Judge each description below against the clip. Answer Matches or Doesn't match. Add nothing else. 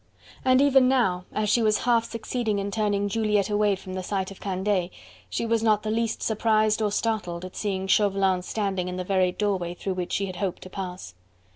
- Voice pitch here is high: Matches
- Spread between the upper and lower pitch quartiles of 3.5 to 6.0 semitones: Doesn't match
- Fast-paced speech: Matches